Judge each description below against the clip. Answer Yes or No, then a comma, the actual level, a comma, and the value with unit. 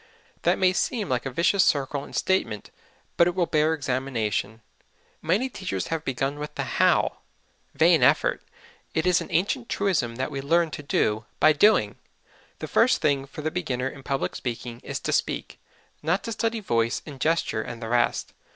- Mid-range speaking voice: Yes, medium, 150 Hz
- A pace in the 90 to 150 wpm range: No, average, 180 wpm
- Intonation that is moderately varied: No, wide, 5.9 semitones